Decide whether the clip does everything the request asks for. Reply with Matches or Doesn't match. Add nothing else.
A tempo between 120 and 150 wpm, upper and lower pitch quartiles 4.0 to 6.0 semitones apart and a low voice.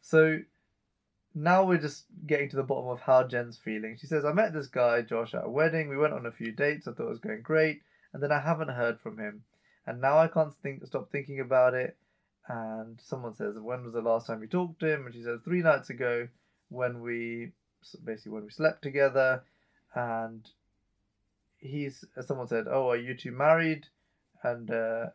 Doesn't match